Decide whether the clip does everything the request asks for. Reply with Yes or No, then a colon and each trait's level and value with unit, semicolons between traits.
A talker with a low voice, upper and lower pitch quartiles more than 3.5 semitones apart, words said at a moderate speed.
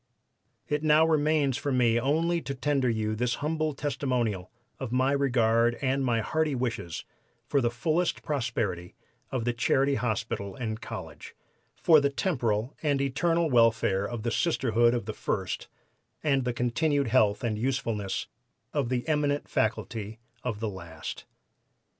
Yes: low, 125 Hz; average, 4.2 semitones; average, 145 wpm